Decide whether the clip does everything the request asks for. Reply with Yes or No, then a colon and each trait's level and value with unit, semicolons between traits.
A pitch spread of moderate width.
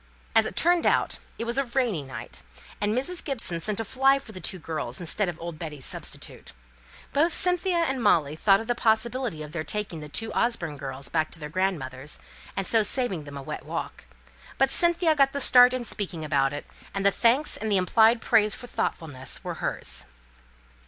No: wide, 8.2 semitones